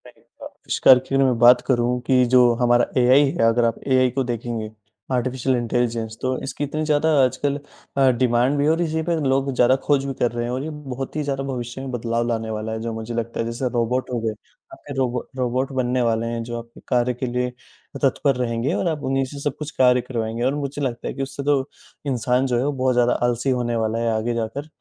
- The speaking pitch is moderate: No, low, 125 Hz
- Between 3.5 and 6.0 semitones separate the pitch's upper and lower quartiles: No, narrow, 2.4 semitones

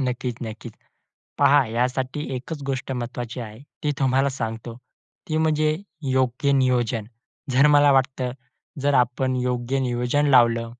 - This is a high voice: No, low, 130 Hz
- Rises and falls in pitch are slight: Yes, narrow, 2.3 semitones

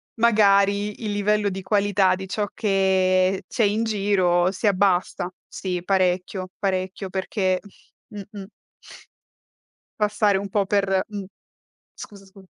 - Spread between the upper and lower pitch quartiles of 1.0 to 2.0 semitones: Yes, narrow, 1.6 semitones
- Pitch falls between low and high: No, high, 195 Hz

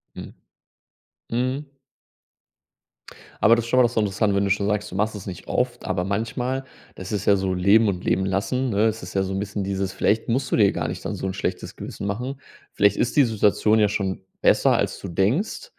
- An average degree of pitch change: Yes, average, 3.3 semitones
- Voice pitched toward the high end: No, low, 105 Hz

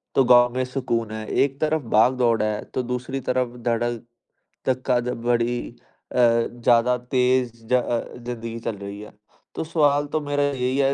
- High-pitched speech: No, low, 125 Hz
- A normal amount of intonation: No, narrow, 1.7 semitones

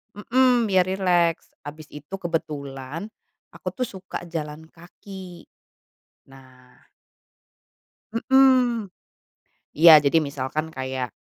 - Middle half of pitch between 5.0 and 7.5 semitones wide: Yes, wide, 5.4 semitones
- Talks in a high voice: No, medium, 165 Hz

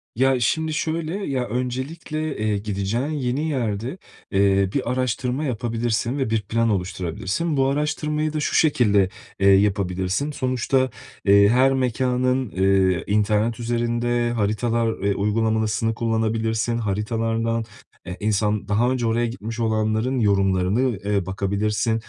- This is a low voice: Yes, low, 115 Hz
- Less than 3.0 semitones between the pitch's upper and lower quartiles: No, average, 3.7 semitones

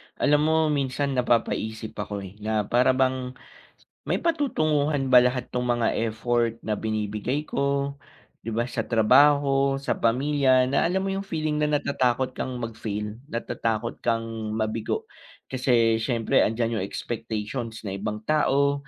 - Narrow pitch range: No, average, 3.8 semitones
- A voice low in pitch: Yes, low, 125 Hz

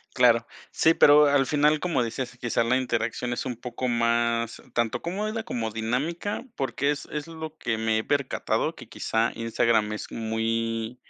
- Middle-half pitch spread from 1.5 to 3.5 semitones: No, average, 4.0 semitones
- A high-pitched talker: No, low, 120 Hz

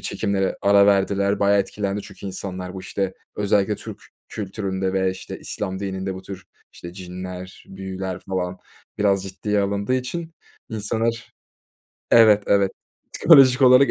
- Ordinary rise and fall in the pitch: No, narrow, 1.7 semitones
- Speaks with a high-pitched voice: No, low, 100 Hz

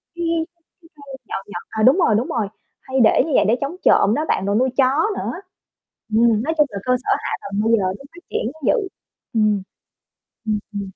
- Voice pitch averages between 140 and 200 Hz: No, high, 230 Hz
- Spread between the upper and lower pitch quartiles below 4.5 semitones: No, average, 5.1 semitones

